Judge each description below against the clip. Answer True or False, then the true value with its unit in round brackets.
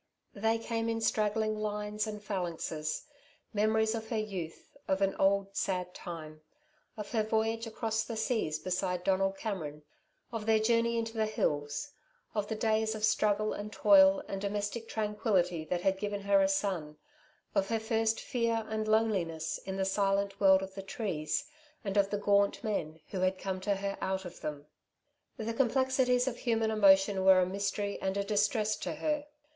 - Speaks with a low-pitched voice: False (205 Hz)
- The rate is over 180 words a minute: False (175 wpm)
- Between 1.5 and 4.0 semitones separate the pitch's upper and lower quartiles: True (2.5 semitones)